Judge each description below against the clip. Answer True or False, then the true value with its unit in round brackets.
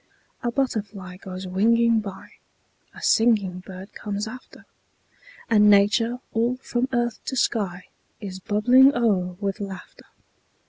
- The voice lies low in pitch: False (210 Hz)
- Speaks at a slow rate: True (125 wpm)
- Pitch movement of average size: True (3.6 semitones)